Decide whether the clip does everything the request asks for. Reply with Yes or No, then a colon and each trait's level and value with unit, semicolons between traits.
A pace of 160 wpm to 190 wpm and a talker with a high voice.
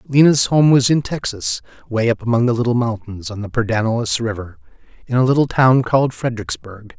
No: average, 180 wpm; low, 115 Hz